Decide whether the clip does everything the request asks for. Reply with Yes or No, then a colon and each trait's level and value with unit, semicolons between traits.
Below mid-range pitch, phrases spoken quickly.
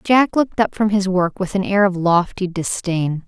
No: high, 190 Hz; fast, 220 wpm